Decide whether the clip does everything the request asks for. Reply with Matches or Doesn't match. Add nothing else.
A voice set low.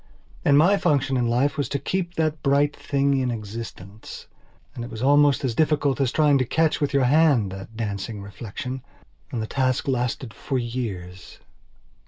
Matches